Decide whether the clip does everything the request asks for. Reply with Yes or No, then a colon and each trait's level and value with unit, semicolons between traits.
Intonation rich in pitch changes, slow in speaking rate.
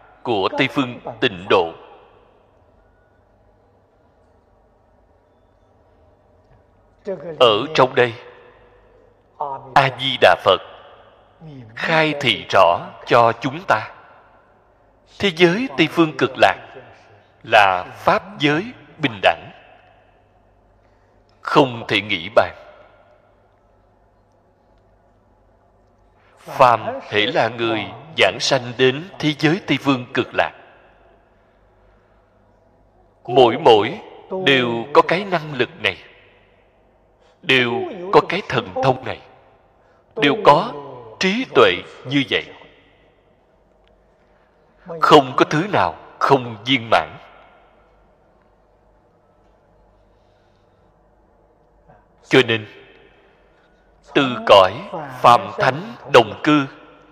Yes: wide, 6.7 semitones; slow, 85 wpm